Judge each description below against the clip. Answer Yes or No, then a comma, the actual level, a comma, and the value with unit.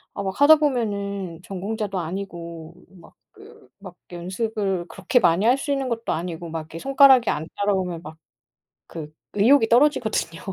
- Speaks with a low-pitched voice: No, high, 200 Hz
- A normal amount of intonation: No, wide, 5.9 semitones